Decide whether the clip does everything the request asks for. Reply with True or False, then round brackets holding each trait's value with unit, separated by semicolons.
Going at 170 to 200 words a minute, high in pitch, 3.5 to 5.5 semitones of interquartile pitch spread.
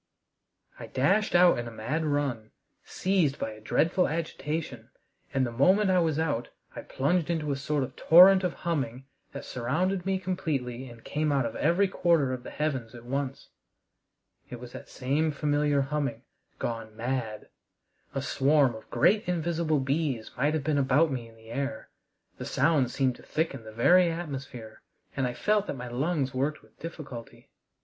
False (175 wpm; 140 Hz; 4.7 semitones)